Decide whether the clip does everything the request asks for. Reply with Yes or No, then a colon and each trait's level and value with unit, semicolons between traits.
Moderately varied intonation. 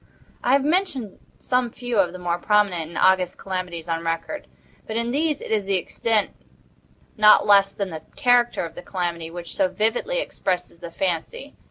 No: wide, 5.7 semitones